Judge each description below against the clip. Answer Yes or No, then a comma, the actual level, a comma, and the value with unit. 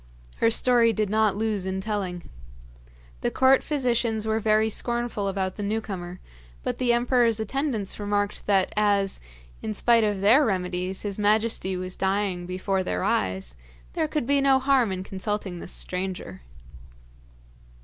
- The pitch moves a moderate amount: Yes, average, 3.4 semitones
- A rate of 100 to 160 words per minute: Yes, average, 150 wpm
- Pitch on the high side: Yes, high, 205 Hz